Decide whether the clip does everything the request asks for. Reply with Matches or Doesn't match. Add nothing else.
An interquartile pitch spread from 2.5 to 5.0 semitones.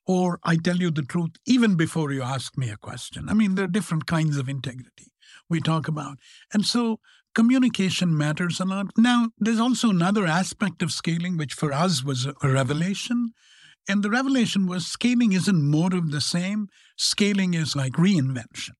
Doesn't match